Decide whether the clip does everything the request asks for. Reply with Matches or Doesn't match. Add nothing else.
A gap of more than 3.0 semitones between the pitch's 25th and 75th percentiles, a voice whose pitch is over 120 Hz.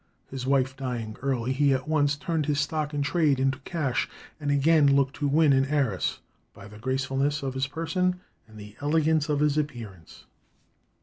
Doesn't match